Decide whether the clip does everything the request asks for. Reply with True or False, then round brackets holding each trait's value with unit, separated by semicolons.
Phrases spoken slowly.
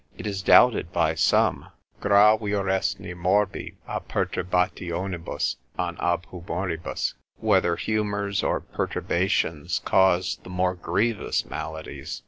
True (105 wpm)